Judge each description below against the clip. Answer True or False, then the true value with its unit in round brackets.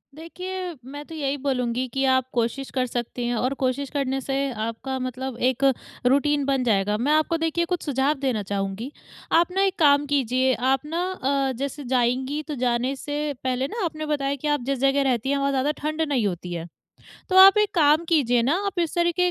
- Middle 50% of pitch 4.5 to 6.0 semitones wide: False (3.3 semitones)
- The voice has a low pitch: False (275 Hz)